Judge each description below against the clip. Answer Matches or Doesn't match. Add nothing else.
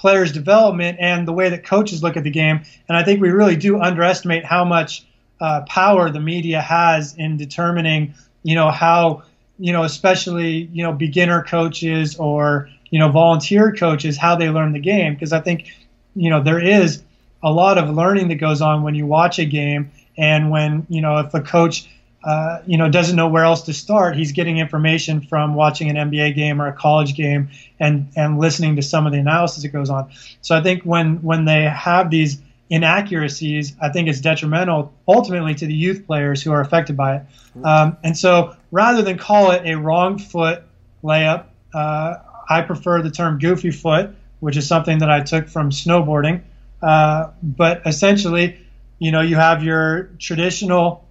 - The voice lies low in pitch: Doesn't match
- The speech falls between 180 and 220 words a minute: Matches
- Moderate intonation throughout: Doesn't match